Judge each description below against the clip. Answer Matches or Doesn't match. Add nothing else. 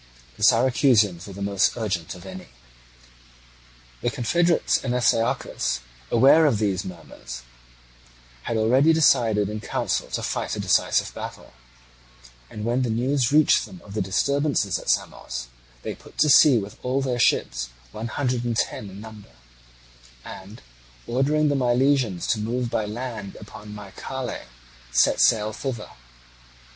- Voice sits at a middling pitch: Doesn't match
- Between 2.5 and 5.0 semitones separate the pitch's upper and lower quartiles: Matches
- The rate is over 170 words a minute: Doesn't match